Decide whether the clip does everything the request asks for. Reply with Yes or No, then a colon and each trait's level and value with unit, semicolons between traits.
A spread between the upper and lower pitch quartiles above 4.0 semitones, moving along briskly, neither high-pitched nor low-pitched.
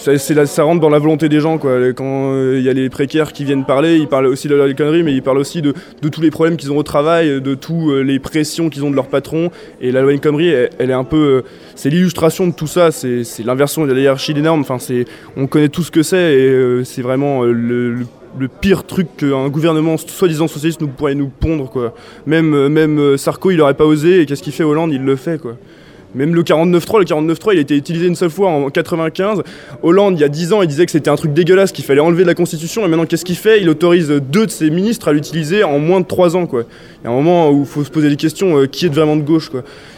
No: average, 3.4 semitones; fast, 280 wpm; medium, 155 Hz